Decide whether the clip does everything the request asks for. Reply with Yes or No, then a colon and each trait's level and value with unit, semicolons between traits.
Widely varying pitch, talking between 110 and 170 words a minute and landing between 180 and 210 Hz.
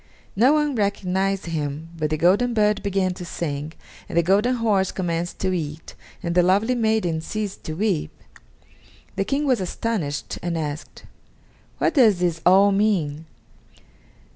No: average, 4.4 semitones; average, 150 wpm; medium, 185 Hz